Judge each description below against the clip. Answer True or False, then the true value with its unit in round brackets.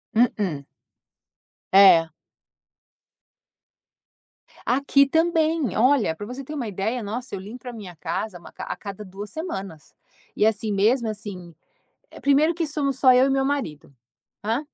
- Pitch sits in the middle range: False (225 Hz)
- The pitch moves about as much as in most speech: False (5.7 semitones)